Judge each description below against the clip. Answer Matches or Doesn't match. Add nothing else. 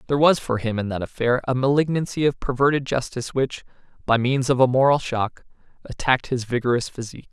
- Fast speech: Doesn't match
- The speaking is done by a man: Matches